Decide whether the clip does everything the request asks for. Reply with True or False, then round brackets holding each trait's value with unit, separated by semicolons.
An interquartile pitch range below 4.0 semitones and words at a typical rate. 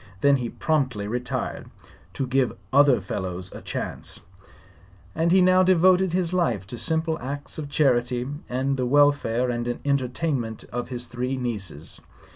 False (4.3 semitones; 150 wpm)